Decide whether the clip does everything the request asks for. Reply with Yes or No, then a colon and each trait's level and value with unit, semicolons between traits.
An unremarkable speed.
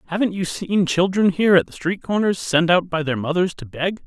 No: fast, 235 wpm